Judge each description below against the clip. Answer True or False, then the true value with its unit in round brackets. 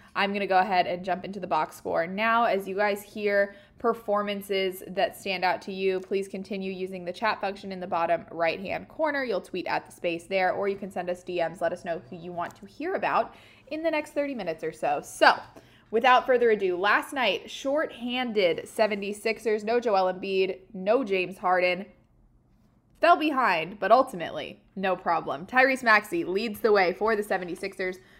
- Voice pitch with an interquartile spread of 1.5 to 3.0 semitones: False (3.4 semitones)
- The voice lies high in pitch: True (195 Hz)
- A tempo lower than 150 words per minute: False (190 wpm)